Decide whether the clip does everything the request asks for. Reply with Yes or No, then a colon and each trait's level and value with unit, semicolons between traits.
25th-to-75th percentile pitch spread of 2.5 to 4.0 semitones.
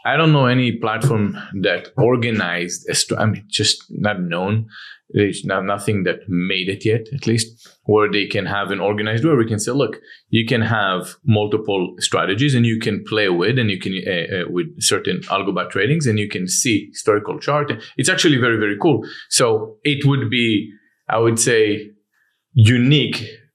Yes: average, 3.7 semitones